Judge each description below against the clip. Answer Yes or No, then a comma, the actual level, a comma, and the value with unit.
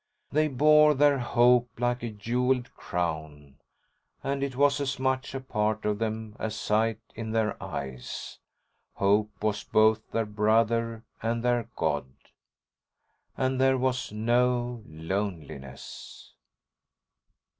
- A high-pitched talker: No, low, 115 Hz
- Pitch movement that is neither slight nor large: Yes, average, 3.2 semitones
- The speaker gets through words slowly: Yes, slow, 120 wpm